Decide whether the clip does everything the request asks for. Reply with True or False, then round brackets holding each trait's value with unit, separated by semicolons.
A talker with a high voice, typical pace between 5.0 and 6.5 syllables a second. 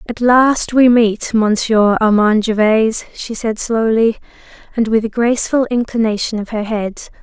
False (225 Hz; 4.6 syllables/s)